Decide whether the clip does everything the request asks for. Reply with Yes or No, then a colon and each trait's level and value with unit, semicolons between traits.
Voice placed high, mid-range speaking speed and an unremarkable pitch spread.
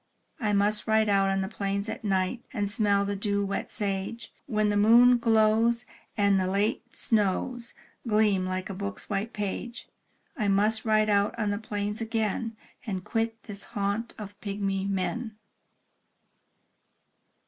No: high, 210 Hz; average, 150 wpm; narrow, 1.9 semitones